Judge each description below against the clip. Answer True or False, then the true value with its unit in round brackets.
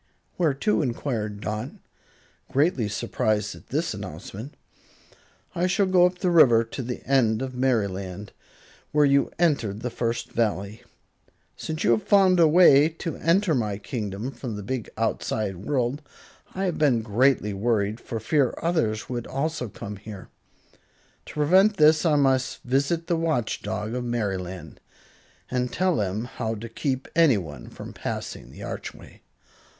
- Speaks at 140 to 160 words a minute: True (150 wpm)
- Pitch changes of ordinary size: False (6.2 semitones)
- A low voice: True (125 Hz)